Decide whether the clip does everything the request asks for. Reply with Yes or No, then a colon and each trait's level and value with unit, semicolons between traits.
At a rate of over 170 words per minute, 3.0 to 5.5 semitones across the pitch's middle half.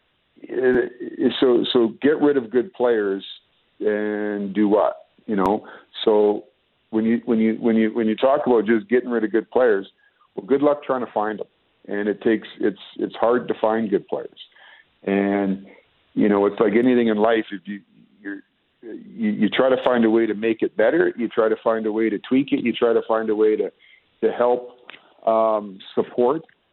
Yes: average, 200 wpm; average, 3.7 semitones